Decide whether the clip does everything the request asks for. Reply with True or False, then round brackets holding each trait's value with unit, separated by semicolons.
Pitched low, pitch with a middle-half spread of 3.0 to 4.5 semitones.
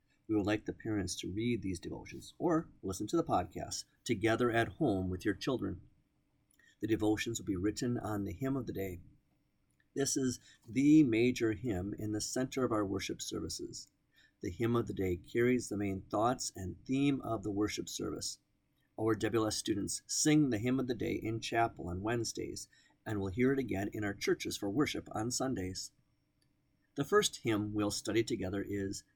True (110 Hz; 3.6 semitones)